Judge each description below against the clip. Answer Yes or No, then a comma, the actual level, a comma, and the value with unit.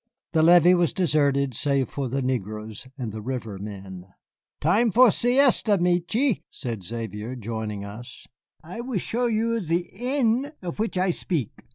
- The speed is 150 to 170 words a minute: Yes, average, 155 wpm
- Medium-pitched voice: Yes, medium, 155 Hz